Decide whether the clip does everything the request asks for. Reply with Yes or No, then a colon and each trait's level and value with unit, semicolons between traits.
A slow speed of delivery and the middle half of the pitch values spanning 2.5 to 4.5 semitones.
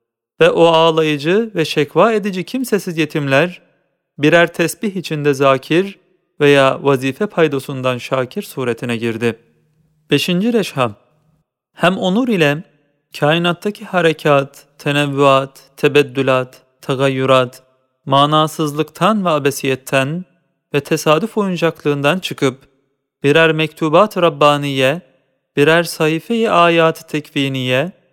Yes: slow, 90 wpm; average, 4.0 semitones